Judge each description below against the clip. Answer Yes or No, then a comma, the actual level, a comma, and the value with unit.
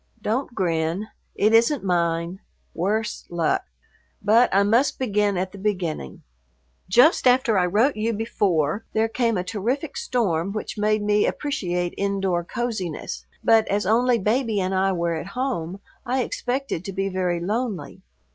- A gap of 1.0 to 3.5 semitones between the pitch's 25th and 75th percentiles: No, average, 4.3 semitones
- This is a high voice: Yes, high, 205 Hz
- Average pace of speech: Yes, average, 150 wpm